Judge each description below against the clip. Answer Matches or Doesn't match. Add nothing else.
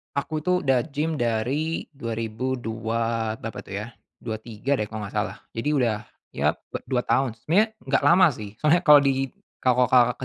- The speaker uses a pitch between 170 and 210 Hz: Doesn't match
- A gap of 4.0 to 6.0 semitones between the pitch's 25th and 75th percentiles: Matches